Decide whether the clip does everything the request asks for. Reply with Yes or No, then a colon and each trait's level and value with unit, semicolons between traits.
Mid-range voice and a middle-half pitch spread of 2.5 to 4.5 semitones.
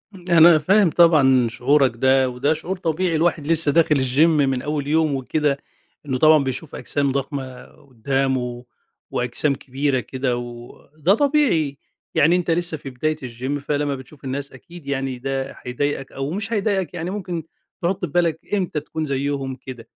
Yes: medium, 145 Hz; average, 3.7 semitones